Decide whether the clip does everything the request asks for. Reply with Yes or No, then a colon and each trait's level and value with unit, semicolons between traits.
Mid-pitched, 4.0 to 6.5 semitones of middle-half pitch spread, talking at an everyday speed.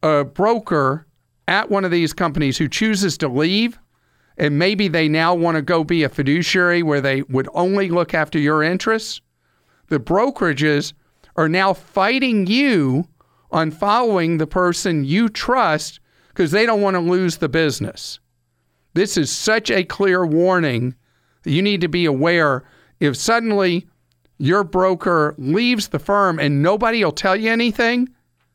Yes: medium, 170 Hz; average, 4.9 semitones; average, 155 wpm